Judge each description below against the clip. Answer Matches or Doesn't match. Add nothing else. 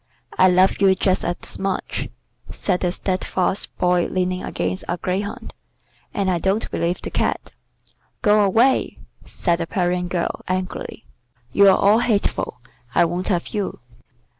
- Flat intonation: Matches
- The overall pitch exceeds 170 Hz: Matches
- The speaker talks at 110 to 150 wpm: Matches